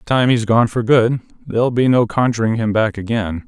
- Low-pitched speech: Yes, low, 115 Hz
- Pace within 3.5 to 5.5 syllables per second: No, 5.7 syllables/s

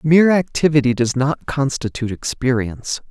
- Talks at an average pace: No, slow, 115 wpm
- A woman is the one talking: No, male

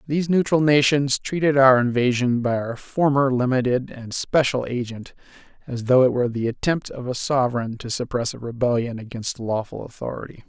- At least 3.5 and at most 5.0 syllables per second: No, 5.3 syllables/s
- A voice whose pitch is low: Yes, low, 130 Hz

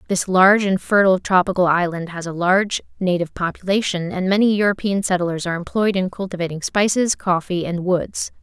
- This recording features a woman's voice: Yes, female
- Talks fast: No, average, 165 wpm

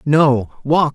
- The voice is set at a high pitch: No, medium, 145 Hz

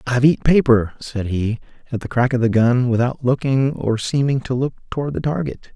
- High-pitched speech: No, low, 125 Hz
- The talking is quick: Yes, fast, 210 wpm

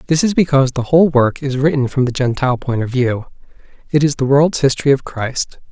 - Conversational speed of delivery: No, fast, 210 wpm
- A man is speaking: Yes, male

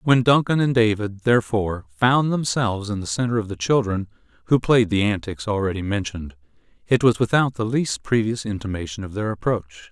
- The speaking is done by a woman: No, male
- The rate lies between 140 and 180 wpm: Yes, average, 175 wpm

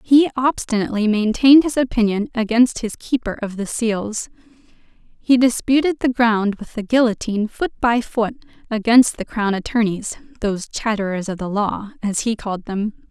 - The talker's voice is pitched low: No, high, 225 Hz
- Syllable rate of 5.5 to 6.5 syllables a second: No, 4.9 syllables/s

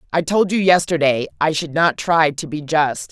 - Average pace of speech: No, fast, 210 wpm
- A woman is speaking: Yes, female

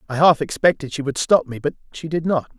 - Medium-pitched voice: Yes, medium, 150 Hz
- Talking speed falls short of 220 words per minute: No, fast, 255 wpm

